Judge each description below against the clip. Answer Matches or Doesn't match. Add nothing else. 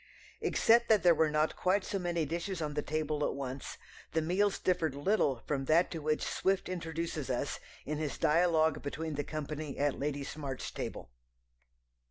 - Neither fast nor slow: Matches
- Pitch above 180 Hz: Doesn't match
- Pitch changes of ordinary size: Matches